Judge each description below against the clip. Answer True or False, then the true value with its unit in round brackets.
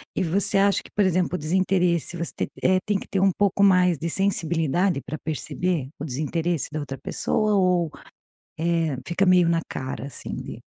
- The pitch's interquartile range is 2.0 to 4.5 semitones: True (2.9 semitones)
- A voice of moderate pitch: True (175 Hz)